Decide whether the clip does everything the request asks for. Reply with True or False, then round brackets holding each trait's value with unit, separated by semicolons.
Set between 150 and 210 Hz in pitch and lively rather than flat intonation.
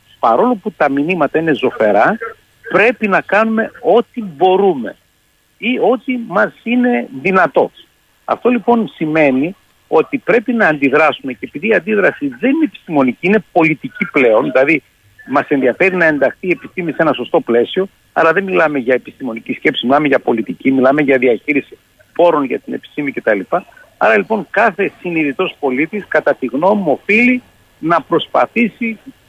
True (190 Hz; 8.1 semitones)